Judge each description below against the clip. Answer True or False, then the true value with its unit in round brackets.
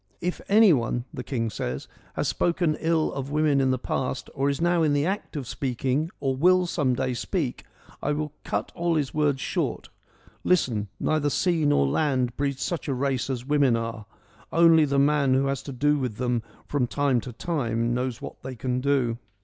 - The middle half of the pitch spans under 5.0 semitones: True (3.4 semitones)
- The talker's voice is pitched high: False (140 Hz)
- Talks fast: True (210 wpm)